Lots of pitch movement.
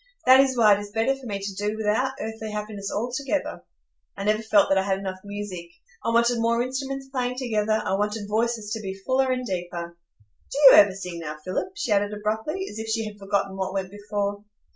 No: average, 3.1 semitones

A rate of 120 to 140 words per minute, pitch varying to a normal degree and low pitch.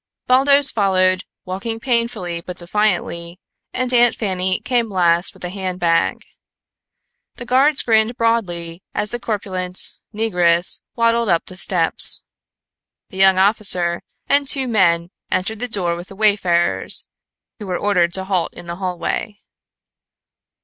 No: slow, 135 wpm; average, 4.5 semitones; high, 190 Hz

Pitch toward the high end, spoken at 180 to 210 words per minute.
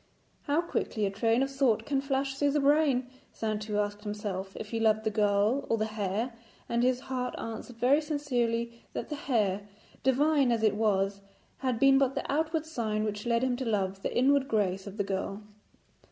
Yes: high, 230 Hz; average, 195 wpm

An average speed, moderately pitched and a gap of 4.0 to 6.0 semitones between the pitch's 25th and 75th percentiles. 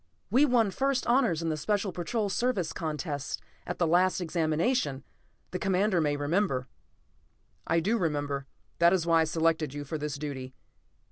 Yes: average, 160 wpm; medium, 165 Hz; average, 4.8 semitones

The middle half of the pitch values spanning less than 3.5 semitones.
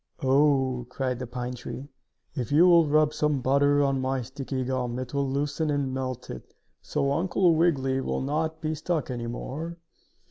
Yes: average, 2.7 semitones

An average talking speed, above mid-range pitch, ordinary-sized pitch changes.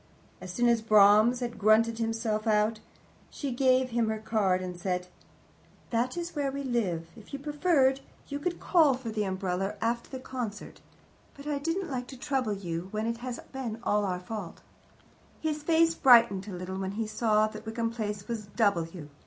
Yes: average, 185 wpm; high, 225 Hz; average, 4.2 semitones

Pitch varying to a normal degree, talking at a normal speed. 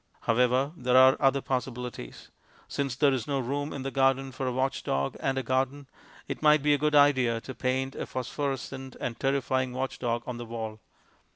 No: narrow, 1.7 semitones; average, 185 wpm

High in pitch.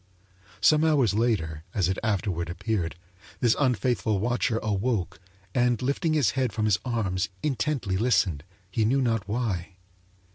No: low, 110 Hz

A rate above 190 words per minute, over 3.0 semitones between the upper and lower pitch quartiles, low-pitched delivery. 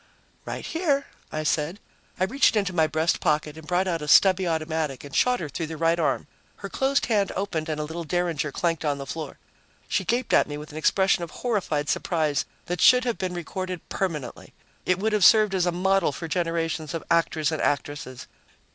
No: fast, 205 wpm; average, 3.6 semitones; medium, 170 Hz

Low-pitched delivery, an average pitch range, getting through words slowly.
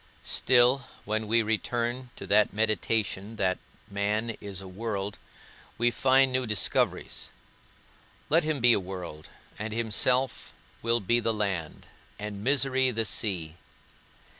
Yes: low, 110 Hz; average, 3.2 semitones; slow, 130 wpm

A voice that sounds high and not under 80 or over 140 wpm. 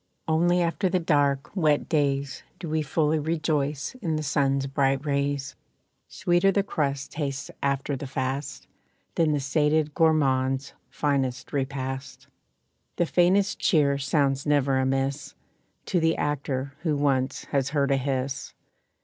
No: medium, 140 Hz; slow, 135 wpm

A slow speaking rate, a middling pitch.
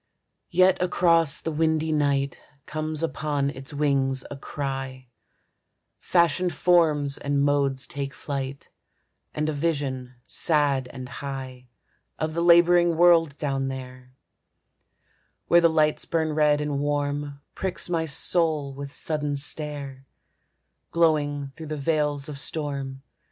Yes: slow, 125 wpm; medium, 145 Hz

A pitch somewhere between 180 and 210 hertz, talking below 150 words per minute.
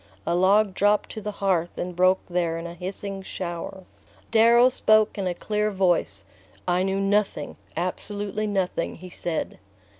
No: high, 190 Hz; average, 155 wpm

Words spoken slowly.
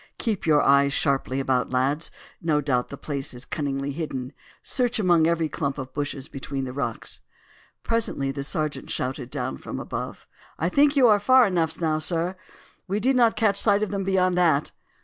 No: average, 190 wpm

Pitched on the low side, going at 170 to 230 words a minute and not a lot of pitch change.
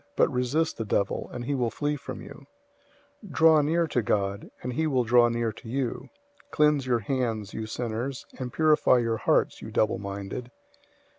No: low, 125 Hz; average, 180 wpm; average, 4.3 semitones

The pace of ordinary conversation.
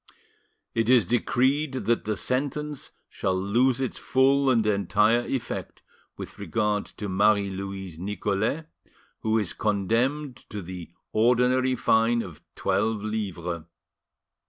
No: slow, 120 wpm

